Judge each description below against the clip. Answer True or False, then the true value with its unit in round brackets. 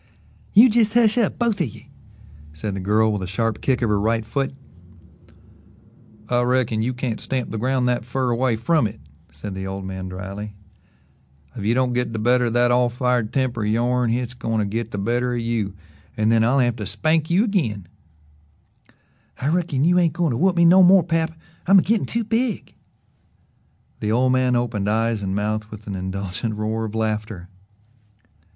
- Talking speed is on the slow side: False (195 wpm)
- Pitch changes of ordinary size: True (4.0 semitones)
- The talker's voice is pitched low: True (120 Hz)